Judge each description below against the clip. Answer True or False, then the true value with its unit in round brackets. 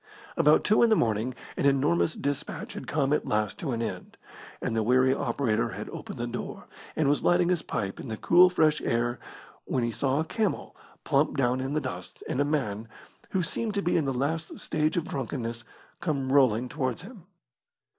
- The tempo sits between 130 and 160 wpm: False (200 wpm)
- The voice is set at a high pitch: False (135 Hz)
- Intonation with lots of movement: False (4.8 semitones)